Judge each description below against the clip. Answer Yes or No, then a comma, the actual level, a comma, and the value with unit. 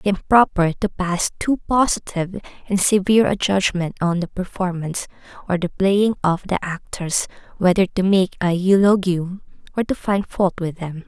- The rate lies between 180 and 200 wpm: No, average, 170 wpm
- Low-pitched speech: No, medium, 185 Hz